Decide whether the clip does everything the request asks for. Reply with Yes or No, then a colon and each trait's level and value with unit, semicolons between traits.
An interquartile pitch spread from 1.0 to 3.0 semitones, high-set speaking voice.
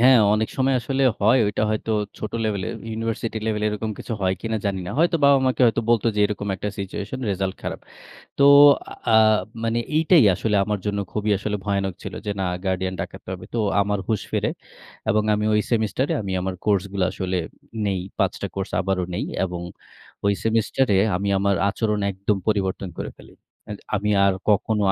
No: narrow, 2.4 semitones; low, 105 Hz